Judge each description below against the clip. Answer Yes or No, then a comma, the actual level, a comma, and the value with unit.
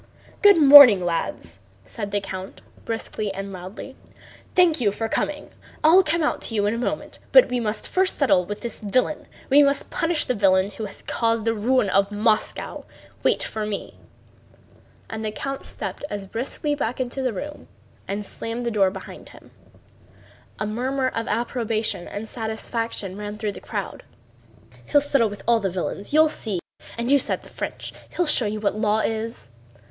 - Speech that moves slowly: No, average, 180 wpm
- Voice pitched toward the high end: Yes, high, 225 Hz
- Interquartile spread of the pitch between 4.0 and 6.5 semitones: Yes, average, 4.4 semitones